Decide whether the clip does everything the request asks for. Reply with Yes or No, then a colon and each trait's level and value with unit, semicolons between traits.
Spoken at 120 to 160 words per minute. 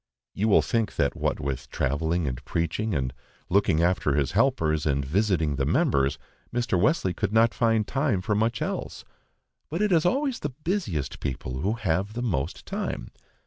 No: average, 175 wpm